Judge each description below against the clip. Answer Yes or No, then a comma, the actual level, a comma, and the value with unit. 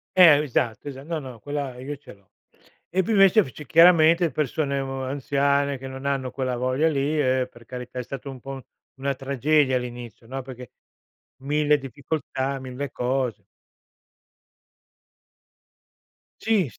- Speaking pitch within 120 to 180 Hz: Yes, low, 135 Hz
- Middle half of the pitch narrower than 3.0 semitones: Yes, narrow, 2.5 semitones